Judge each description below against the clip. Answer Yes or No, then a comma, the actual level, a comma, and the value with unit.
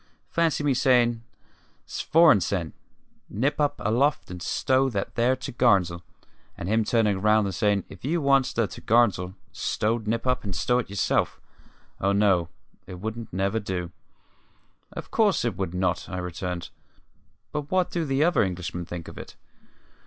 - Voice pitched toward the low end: Yes, low, 110 Hz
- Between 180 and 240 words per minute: No, average, 155 wpm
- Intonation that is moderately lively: No, wide, 5.8 semitones